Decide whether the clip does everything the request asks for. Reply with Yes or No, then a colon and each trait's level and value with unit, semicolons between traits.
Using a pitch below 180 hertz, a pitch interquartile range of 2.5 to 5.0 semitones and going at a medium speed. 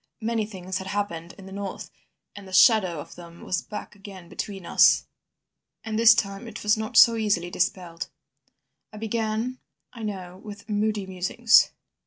No: high, 205 Hz; average, 2.9 semitones; average, 165 wpm